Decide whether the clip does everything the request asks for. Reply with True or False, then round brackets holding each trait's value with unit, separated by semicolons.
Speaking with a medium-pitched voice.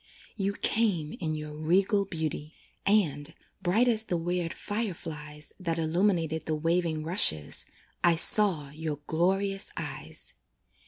True (165 Hz)